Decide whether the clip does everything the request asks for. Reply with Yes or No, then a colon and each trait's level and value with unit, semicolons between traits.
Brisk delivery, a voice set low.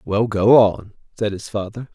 No: average, 185 wpm; low, 105 Hz